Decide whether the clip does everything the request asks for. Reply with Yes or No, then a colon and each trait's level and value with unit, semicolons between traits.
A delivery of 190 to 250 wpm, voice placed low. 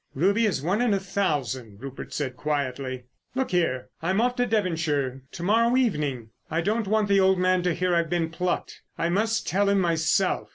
No: average, 195 wpm; medium, 180 Hz